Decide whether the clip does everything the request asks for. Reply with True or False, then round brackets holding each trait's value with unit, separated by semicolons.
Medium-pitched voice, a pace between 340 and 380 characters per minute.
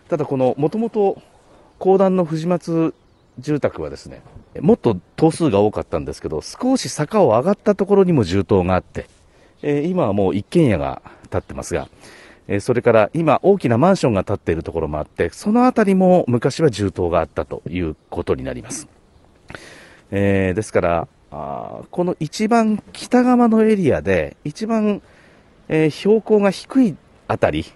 False (160 Hz; 320 characters per minute)